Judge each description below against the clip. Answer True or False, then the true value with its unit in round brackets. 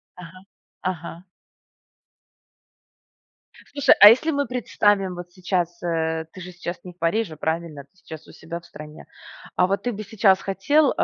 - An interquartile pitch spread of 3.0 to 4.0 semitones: True (3.5 semitones)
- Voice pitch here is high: False (180 Hz)